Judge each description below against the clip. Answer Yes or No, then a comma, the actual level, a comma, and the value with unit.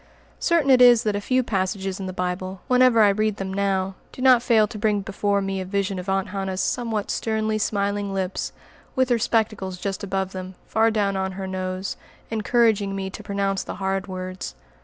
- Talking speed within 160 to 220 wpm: Yes, average, 200 wpm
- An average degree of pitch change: No, narrow, 2.3 semitones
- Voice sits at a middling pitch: No, high, 200 Hz